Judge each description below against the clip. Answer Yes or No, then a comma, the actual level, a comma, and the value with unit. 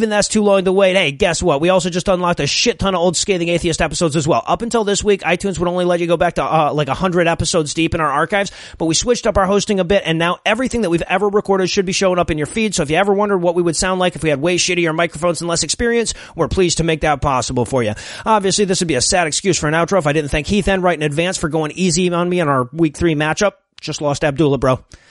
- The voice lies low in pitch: No, medium, 175 Hz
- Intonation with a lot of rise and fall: No, average, 3.2 semitones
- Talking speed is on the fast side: Yes, fast, 300 wpm